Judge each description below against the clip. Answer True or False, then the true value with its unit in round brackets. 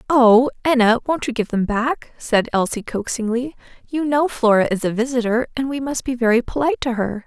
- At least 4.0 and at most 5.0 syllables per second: False (5.5 syllables/s)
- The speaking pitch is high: True (245 Hz)